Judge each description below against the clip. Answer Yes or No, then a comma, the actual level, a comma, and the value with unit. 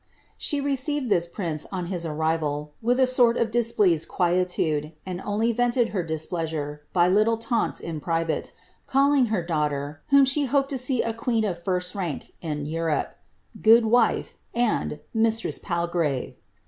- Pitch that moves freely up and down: Yes, wide, 6.4 semitones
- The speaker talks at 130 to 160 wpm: No, average, 170 wpm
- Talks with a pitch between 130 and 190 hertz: Yes, medium, 185 Hz